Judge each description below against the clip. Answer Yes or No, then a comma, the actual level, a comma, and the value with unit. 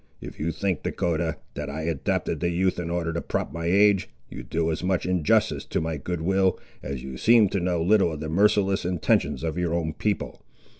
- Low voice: Yes, very low, 85 Hz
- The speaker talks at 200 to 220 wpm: Yes, fast, 205 wpm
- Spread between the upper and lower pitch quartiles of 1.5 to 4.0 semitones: Yes, average, 2.9 semitones